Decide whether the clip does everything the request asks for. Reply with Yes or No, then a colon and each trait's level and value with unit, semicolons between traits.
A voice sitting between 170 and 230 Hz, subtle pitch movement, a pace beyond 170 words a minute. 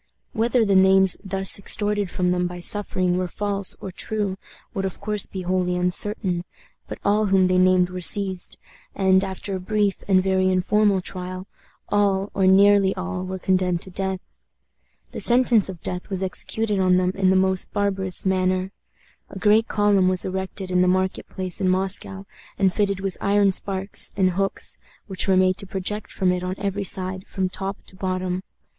Yes: high, 190 Hz; narrow, 1.3 semitones; average, 180 wpm